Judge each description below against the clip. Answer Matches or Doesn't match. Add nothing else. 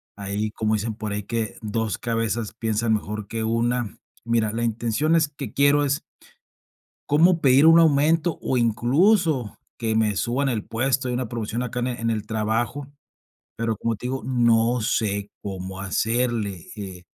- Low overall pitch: Matches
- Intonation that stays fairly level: Doesn't match